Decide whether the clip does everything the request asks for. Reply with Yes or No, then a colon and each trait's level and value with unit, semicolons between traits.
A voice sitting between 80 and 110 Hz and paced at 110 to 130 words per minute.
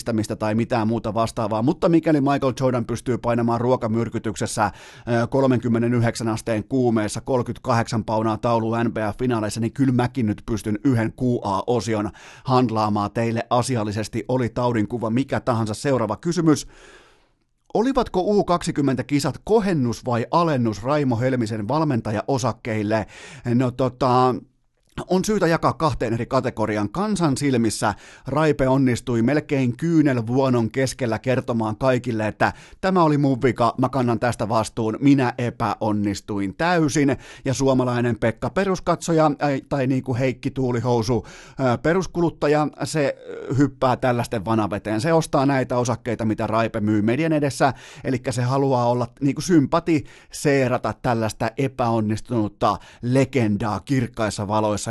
No: low, 125 Hz; average, 120 wpm